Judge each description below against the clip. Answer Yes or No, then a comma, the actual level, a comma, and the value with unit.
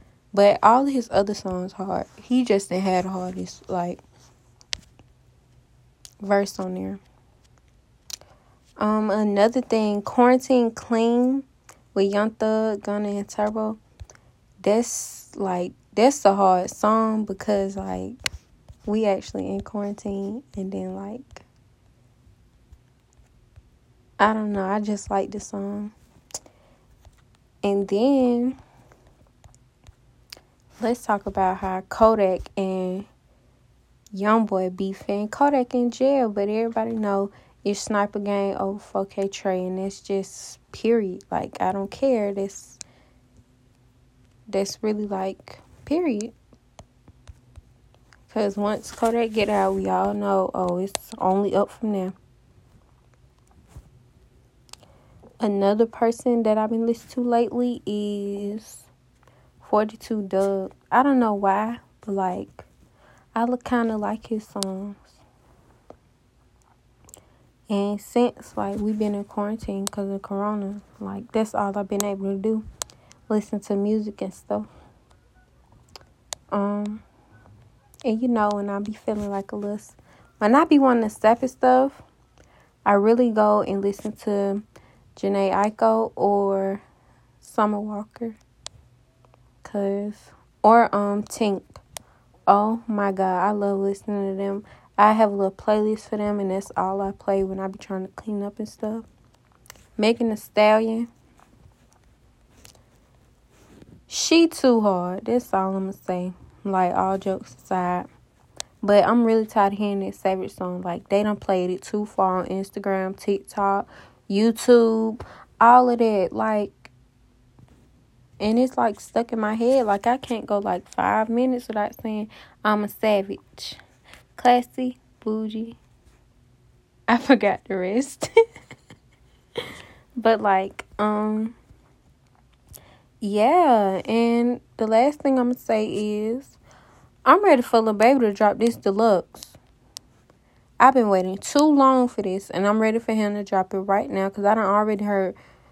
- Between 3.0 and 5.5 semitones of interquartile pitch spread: No, narrow, 2.5 semitones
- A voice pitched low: No, high, 205 Hz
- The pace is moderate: No, slow, 130 wpm